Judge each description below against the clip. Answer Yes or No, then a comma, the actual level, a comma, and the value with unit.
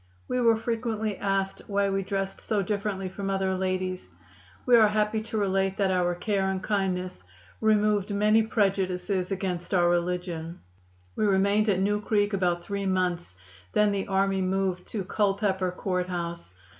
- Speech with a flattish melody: Yes, narrow, 2.1 semitones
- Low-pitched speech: No, high, 195 Hz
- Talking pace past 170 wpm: No, average, 155 wpm